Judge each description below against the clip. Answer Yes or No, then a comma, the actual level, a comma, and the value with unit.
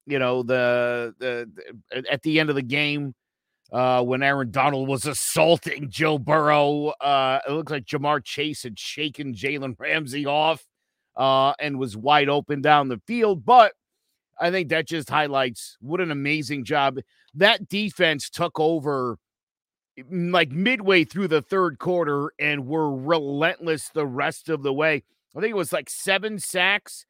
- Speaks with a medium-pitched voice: Yes, medium, 150 Hz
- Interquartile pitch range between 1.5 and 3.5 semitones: Yes, average, 3.1 semitones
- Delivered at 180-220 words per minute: No, average, 160 wpm